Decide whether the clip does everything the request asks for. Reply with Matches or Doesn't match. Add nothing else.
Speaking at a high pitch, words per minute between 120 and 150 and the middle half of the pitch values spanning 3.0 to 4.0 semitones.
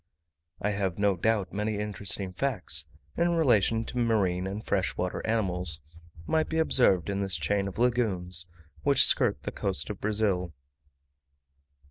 Doesn't match